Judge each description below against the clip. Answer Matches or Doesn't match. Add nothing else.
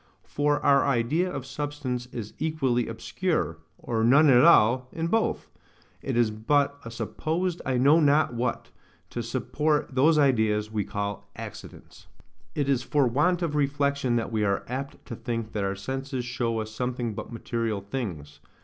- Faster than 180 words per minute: Doesn't match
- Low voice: Matches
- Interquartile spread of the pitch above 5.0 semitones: Doesn't match